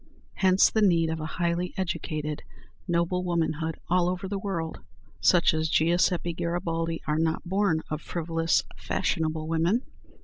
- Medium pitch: Yes, medium, 170 Hz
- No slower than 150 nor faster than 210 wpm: No, average, 140 wpm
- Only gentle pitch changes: Yes, narrow, 2.1 semitones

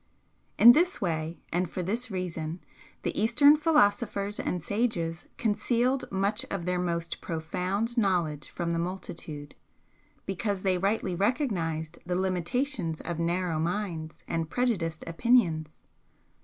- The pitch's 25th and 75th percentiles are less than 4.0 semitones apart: No, average, 4.6 semitones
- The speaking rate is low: Yes, slow, 125 wpm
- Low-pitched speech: No, medium, 185 Hz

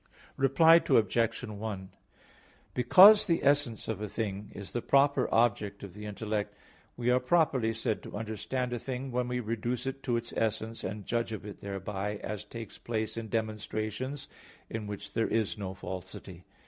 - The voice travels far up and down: No, average, 3.1 semitones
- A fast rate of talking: No, average, 170 wpm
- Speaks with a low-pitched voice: Yes, low, 110 Hz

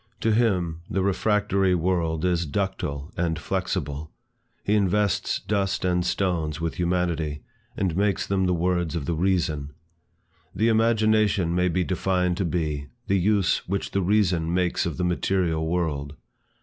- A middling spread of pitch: Yes, average, 3.0 semitones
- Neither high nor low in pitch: No, very low, 90 Hz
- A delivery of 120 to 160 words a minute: Yes, average, 150 wpm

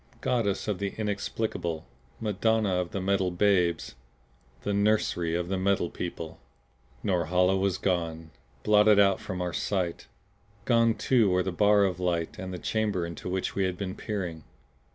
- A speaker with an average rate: Yes, average, 155 wpm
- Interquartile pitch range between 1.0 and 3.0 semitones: Yes, narrow, 2.6 semitones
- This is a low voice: Yes, very low, 95 Hz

